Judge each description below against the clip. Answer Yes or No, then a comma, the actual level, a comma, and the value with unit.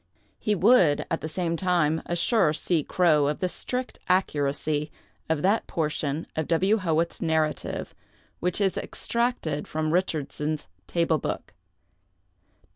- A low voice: No, medium, 165 Hz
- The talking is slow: Yes, slow, 125 wpm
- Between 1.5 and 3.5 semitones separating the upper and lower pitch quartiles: Yes, average, 3.2 semitones